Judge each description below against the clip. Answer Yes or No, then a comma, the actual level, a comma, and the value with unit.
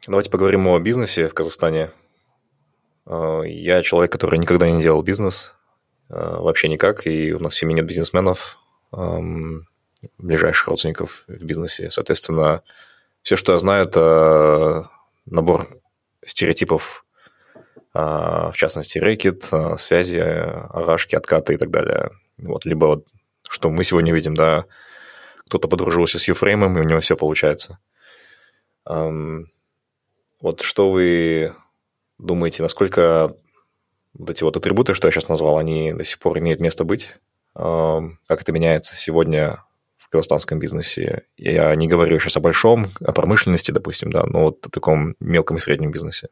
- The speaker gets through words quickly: No, average, 135 wpm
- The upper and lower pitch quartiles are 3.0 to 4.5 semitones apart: No, narrow, 2.5 semitones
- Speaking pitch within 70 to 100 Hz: Yes, very low, 80 Hz